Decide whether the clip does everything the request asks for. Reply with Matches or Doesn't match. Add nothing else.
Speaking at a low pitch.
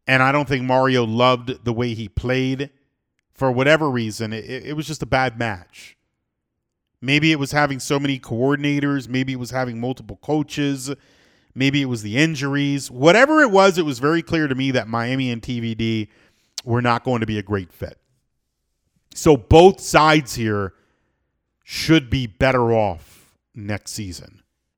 Matches